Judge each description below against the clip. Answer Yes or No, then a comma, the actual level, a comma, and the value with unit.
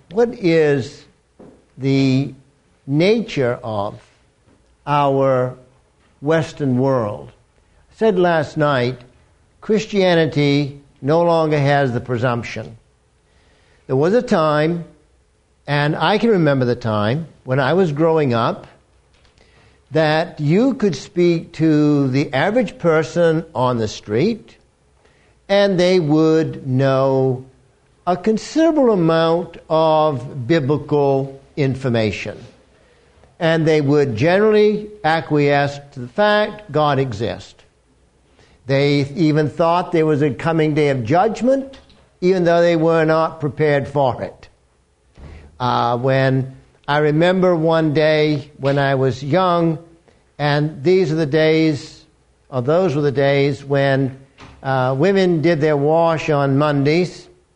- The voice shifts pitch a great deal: No, average, 3.7 semitones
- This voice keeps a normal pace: No, slow, 115 wpm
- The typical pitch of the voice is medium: Yes, medium, 150 Hz